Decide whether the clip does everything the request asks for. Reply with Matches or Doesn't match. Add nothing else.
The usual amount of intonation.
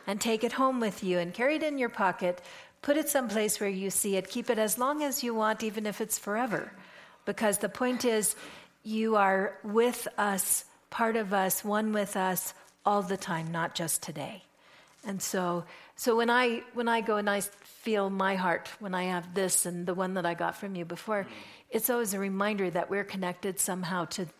Matches